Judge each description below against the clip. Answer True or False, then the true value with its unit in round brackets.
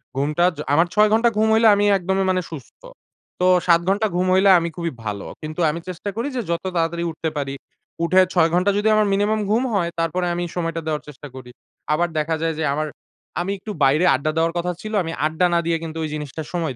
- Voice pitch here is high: False (170 Hz)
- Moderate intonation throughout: True (3.4 semitones)